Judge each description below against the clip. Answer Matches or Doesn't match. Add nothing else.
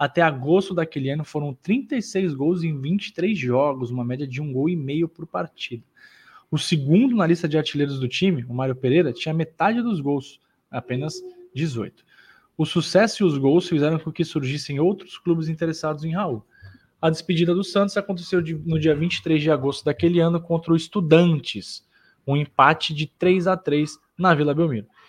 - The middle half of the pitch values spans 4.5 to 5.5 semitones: Doesn't match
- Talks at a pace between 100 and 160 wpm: Doesn't match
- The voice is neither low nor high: Matches